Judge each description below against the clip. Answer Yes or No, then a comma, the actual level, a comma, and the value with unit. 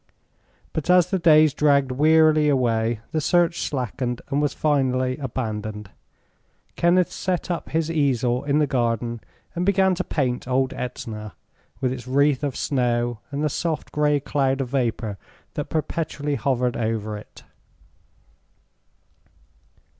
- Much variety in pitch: No, average, 4.1 semitones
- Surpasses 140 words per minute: No, slow, 135 wpm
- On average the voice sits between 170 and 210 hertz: No, low, 135 Hz